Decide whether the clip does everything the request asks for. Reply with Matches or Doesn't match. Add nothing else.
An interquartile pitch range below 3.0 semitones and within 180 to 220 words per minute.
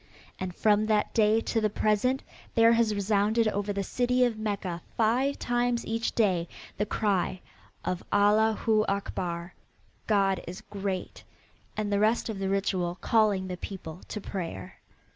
Doesn't match